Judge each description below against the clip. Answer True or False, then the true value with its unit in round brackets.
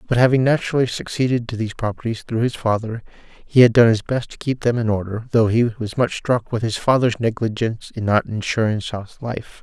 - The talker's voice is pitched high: False (115 Hz)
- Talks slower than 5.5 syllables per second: False (5.6 syllables/s)